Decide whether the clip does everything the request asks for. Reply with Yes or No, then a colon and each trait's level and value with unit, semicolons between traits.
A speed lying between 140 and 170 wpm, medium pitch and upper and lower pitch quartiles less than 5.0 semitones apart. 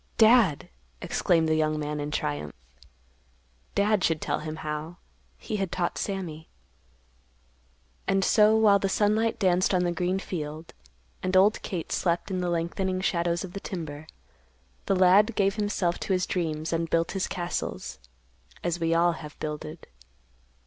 Yes: average, 150 wpm; medium, 175 Hz; average, 3.5 semitones